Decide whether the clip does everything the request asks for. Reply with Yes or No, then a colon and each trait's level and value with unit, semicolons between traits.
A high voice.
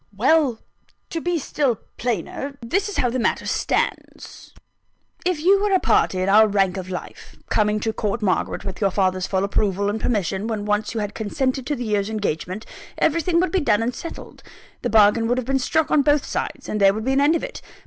Yes: high, 225 Hz